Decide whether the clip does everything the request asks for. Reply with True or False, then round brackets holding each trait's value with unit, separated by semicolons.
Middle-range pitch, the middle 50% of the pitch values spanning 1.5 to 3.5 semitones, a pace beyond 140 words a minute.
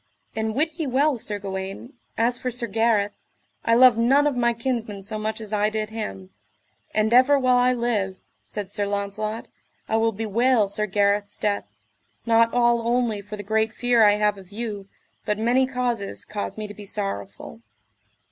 False (220 Hz; 2.8 semitones; 180 wpm)